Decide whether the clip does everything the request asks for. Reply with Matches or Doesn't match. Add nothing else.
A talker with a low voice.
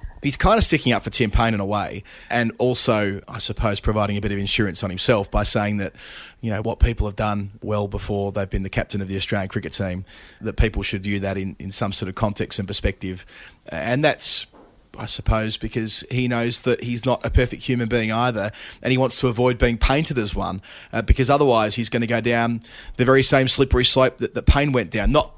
Matches